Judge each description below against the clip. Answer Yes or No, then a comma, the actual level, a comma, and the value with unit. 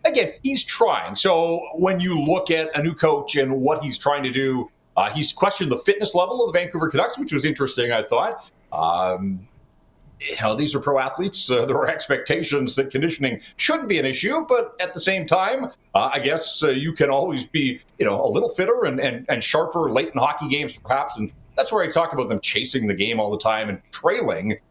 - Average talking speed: No, fast, 220 wpm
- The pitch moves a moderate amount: No, wide, 6.2 semitones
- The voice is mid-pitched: Yes, medium, 155 Hz